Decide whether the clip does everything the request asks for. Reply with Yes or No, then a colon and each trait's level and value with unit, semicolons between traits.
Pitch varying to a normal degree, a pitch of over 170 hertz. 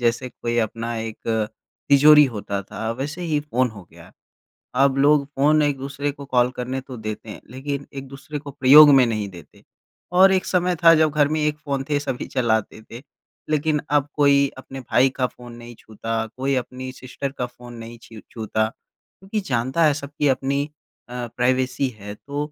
No: average, 3.5 semitones; low, 135 Hz